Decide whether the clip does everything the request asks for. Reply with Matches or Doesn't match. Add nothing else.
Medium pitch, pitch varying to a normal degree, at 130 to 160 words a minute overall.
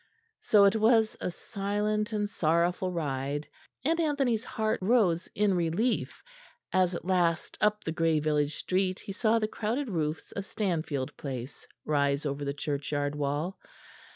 Doesn't match